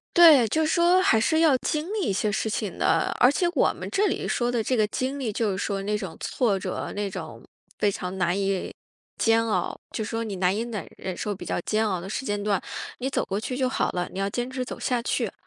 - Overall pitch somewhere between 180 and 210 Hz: No, high, 220 Hz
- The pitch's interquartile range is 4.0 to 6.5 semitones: Yes, average, 4.7 semitones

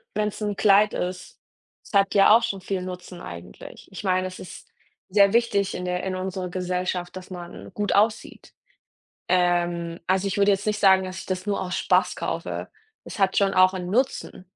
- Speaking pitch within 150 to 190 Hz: Yes, medium, 185 Hz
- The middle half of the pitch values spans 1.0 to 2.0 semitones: Yes, narrow, 1.7 semitones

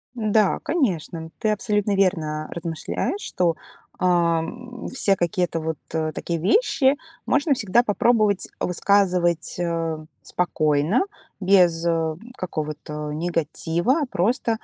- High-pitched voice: No, medium, 180 Hz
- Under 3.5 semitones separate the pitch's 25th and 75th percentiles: No, average, 4.6 semitones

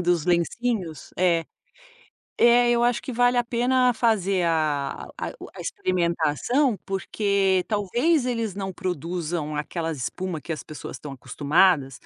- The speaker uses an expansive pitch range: Yes, wide, 6.4 semitones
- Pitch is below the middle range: No, medium, 185 Hz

